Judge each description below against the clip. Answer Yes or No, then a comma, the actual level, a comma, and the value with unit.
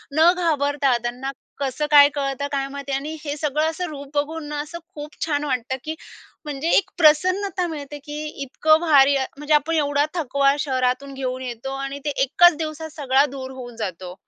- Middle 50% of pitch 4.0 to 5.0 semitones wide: No, narrow, 2.4 semitones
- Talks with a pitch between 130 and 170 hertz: No, very high, 285 Hz